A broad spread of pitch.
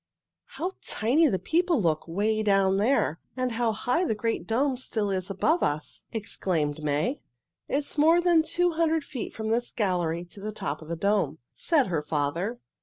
Yes: wide, 8.1 semitones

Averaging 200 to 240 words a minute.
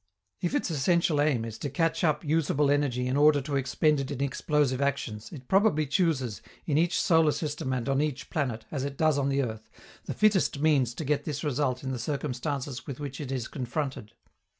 Yes: fast, 205 wpm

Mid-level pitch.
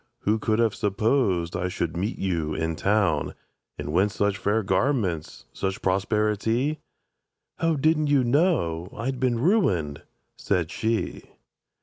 No: low, 105 Hz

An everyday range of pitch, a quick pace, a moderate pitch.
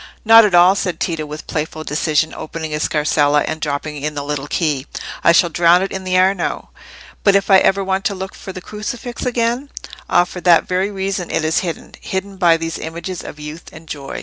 Yes: average, 3.7 semitones; fast, 210 wpm; medium, 175 Hz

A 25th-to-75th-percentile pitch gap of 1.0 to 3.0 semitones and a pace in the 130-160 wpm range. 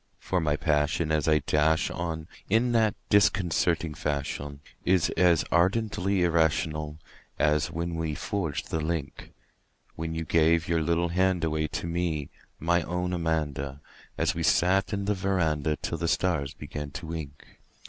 Yes: narrow, 2.6 semitones; average, 150 wpm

